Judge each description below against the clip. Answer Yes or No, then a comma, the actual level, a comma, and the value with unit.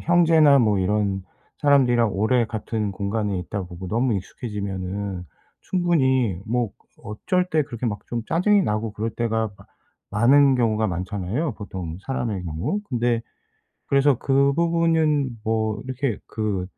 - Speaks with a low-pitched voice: Yes, low, 115 Hz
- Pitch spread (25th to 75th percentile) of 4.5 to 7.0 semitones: Yes, average, 5.2 semitones